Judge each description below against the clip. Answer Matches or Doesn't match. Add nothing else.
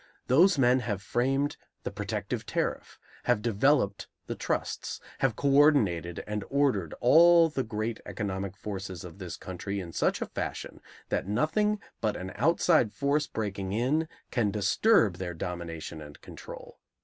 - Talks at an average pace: Matches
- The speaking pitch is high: Doesn't match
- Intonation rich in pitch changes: Matches